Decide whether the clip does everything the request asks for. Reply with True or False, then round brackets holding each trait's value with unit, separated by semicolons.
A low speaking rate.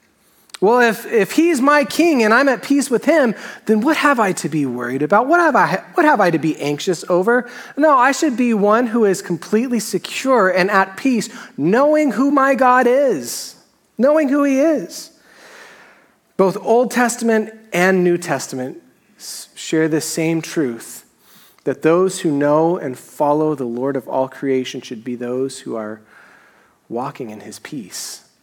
False (170 wpm)